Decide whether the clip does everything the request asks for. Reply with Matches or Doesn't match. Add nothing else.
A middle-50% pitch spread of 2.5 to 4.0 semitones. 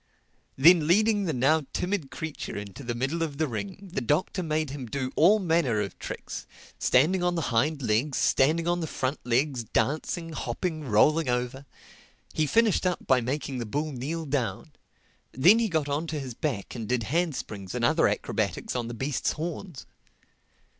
Doesn't match